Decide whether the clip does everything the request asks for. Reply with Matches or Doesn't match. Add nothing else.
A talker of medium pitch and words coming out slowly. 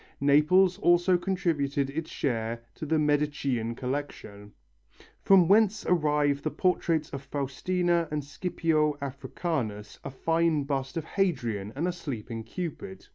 Matches